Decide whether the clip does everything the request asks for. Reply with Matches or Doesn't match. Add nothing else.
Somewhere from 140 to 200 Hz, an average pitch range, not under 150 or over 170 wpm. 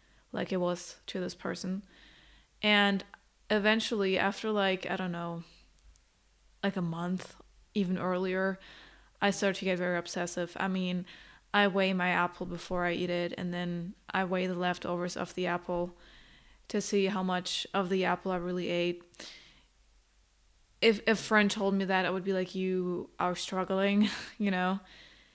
Doesn't match